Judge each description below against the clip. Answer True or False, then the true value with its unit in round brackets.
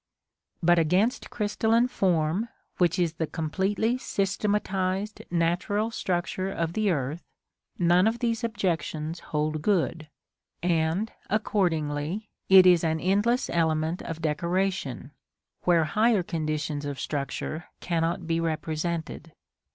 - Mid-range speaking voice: True (175 Hz)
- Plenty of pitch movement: False (4.0 semitones)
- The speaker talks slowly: True (110 wpm)